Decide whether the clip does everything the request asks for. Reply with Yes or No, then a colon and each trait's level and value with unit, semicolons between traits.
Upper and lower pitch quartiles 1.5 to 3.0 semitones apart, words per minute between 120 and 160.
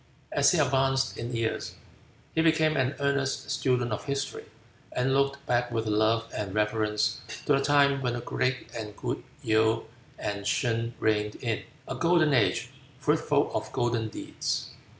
No: average, 3.8 semitones; average, 155 wpm